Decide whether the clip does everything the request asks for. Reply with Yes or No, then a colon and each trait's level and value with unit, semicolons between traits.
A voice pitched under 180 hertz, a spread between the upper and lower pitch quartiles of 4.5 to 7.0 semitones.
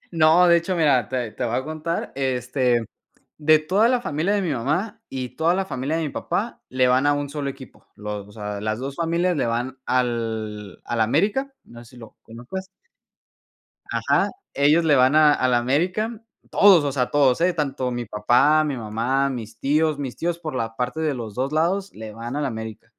Yes: low, 135 Hz; average, 5.0 semitones